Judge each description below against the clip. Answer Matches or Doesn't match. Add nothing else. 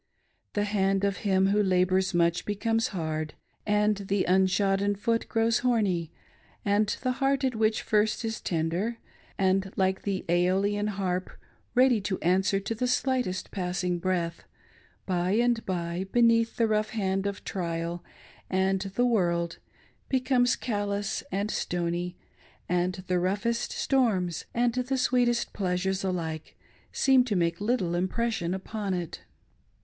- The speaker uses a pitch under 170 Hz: Doesn't match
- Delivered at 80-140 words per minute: Matches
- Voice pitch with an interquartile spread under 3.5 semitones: Doesn't match